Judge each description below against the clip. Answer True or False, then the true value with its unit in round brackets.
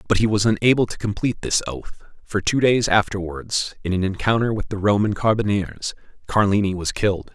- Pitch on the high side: False (100 Hz)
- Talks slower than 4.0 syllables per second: False (5.5 syllables/s)